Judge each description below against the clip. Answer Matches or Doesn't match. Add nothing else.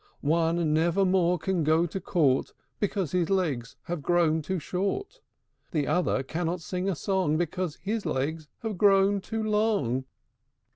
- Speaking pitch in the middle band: Matches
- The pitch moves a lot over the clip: Doesn't match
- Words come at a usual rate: Matches